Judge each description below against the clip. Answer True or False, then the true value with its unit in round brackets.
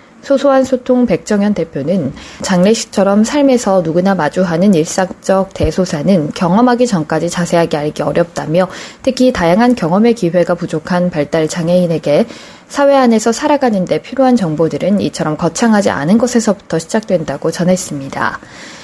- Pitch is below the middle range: False (185 Hz)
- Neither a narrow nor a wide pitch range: False (6.0 semitones)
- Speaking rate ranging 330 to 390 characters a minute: True (355 characters per minute)